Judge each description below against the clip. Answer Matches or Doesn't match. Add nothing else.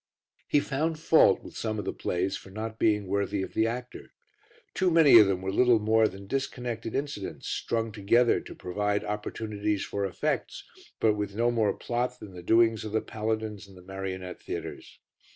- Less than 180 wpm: Doesn't match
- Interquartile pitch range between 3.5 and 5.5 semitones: Doesn't match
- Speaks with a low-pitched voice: Matches